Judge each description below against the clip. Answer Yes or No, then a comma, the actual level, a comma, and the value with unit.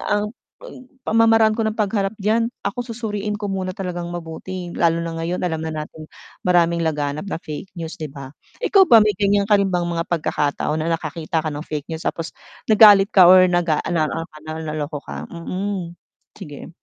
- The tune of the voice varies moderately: Yes, average, 4.2 semitones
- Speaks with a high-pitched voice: No, medium, 175 Hz